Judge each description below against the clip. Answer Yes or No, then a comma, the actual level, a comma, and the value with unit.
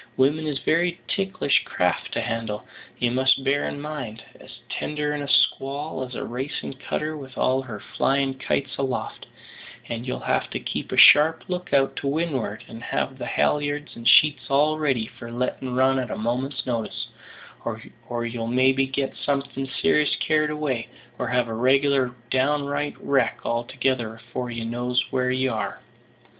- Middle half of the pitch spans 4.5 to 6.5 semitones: No, average, 2.9 semitones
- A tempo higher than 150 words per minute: Yes, average, 170 wpm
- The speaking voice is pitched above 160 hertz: No, low, 135 Hz